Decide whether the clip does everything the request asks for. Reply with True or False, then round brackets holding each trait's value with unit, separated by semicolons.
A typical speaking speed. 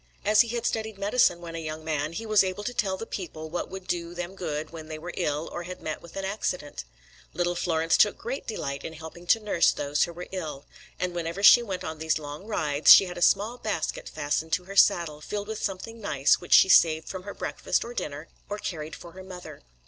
False (235 wpm)